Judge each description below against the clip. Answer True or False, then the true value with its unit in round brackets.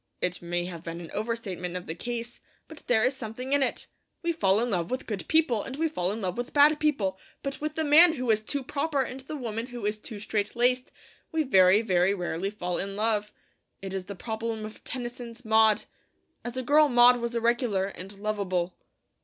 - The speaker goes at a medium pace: False (215 wpm)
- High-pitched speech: True (225 Hz)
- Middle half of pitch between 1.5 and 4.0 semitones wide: False (4.7 semitones)